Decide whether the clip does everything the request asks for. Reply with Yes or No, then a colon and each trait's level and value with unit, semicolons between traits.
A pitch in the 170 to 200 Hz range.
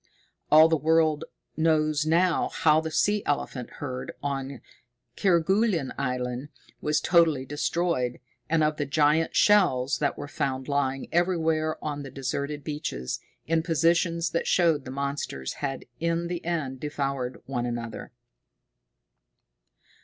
No: medium, 150 Hz